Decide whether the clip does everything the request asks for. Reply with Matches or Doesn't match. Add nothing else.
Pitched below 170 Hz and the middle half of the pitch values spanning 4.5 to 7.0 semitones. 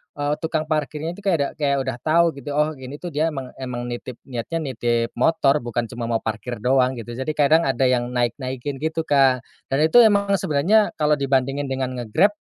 Doesn't match